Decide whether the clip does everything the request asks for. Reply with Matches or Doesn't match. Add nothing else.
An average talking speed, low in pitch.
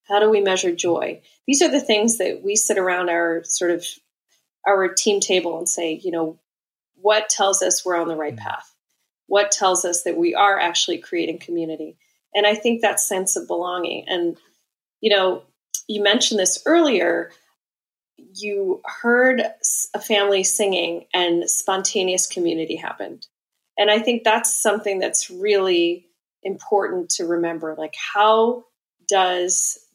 Doesn't match